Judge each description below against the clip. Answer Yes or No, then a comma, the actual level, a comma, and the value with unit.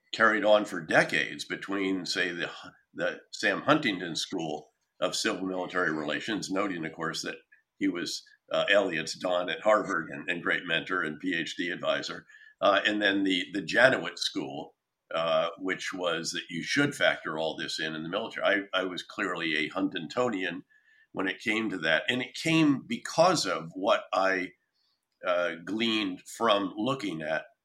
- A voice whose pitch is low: Yes, low, 125 Hz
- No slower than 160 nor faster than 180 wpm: Yes, average, 165 wpm